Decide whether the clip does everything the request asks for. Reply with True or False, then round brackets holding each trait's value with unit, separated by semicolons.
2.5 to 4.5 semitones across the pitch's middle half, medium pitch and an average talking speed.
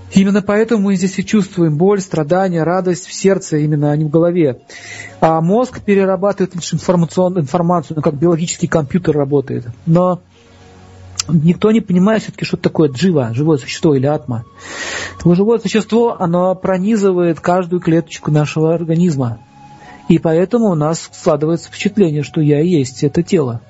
True (3.8 semitones; 170 Hz; 150 wpm)